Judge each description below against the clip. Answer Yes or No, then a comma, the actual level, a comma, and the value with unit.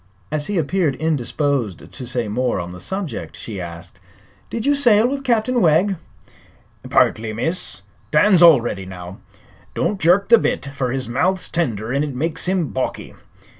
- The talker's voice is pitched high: No, medium, 150 Hz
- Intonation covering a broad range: Yes, wide, 8.3 semitones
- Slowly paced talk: No, average, 160 wpm